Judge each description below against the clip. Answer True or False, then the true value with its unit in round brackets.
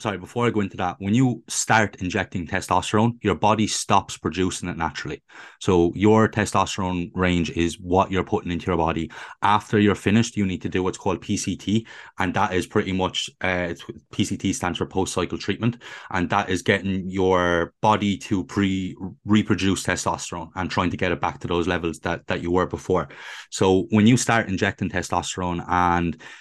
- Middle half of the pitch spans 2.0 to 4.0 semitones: True (2.9 semitones)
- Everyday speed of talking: True (180 wpm)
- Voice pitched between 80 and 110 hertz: True (95 Hz)